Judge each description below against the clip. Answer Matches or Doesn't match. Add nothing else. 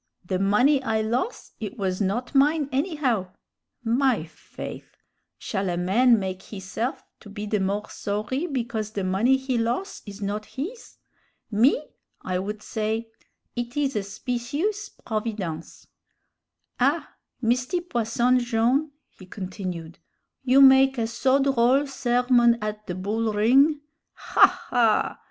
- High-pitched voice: Matches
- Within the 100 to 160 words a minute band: Matches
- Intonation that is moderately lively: Matches